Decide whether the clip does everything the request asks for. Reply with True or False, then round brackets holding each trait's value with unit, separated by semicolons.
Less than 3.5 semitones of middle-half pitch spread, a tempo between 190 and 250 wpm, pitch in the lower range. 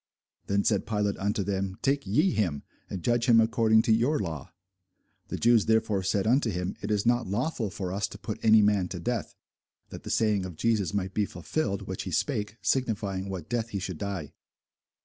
True (2.9 semitones; 200 wpm; 105 Hz)